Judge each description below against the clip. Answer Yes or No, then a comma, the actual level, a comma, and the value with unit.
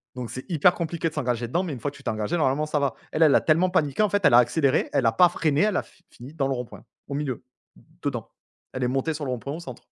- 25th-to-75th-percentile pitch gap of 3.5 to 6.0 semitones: Yes, average, 4.1 semitones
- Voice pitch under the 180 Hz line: Yes, medium, 140 Hz